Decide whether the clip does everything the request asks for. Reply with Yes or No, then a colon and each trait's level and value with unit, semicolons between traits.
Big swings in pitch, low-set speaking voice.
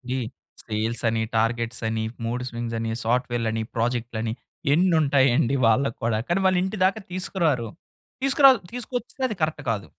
Yes: wide, 7.7 semitones; low, 120 Hz